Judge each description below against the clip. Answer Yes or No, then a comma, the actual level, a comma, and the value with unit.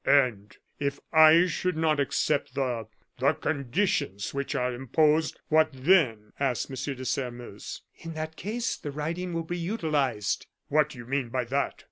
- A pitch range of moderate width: Yes, average, 3.9 semitones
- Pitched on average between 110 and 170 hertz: Yes, medium, 140 Hz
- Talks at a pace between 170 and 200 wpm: No, average, 160 wpm